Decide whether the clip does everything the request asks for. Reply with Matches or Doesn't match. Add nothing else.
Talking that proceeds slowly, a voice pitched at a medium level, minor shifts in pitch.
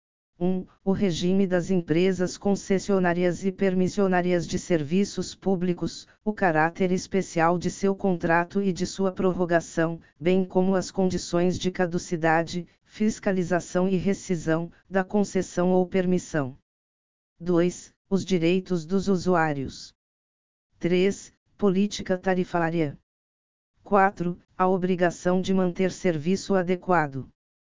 Matches